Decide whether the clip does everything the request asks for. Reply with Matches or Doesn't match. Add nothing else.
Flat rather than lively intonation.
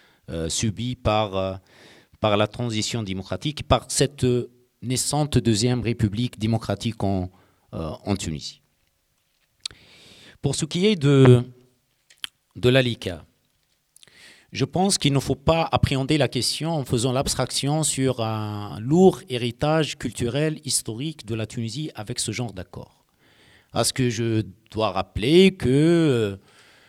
Doesn't match